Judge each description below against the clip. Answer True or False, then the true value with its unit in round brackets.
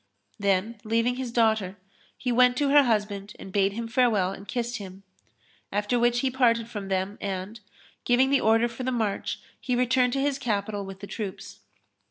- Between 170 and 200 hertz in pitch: False (230 Hz)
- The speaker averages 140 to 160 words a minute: False (185 wpm)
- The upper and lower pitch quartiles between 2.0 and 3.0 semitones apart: False (3.6 semitones)